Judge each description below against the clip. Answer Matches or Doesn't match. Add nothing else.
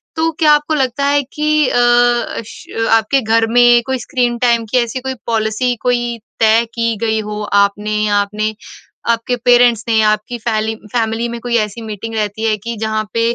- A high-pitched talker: Matches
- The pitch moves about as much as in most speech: Doesn't match